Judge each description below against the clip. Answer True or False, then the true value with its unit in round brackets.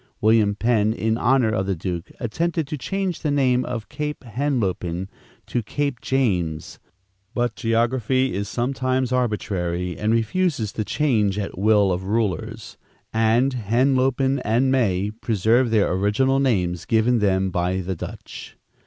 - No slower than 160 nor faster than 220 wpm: False (140 wpm)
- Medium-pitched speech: False (115 Hz)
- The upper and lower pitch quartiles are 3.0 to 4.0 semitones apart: False (4.4 semitones)